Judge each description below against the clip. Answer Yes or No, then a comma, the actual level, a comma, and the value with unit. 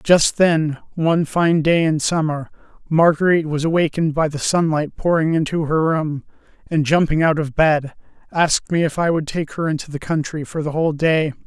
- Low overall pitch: No, medium, 160 Hz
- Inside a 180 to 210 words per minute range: Yes, average, 190 wpm